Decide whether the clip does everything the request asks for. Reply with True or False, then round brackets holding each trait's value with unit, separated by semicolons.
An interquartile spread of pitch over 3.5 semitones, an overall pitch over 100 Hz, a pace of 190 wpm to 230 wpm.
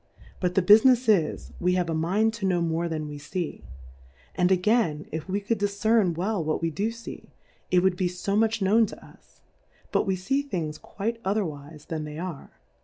True (4.6 semitones; 185 Hz; 200 wpm)